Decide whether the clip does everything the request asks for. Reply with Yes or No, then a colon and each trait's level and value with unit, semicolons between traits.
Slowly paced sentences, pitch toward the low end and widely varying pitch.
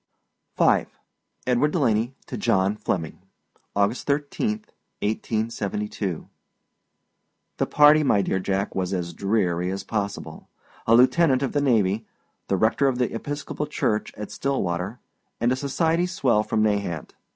Yes: slow, 130 wpm; low, 110 Hz; wide, 5.7 semitones